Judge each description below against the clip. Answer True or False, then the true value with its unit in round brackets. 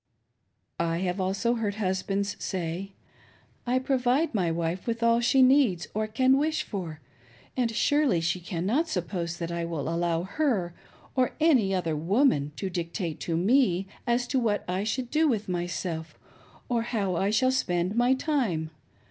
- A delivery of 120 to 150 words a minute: False (165 wpm)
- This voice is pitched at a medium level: False (200 Hz)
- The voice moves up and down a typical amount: False (6.2 semitones)